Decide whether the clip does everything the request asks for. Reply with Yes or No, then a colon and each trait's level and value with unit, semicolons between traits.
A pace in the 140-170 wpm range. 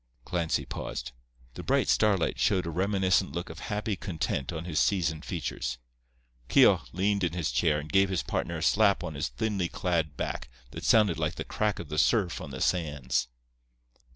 No: average, 180 wpm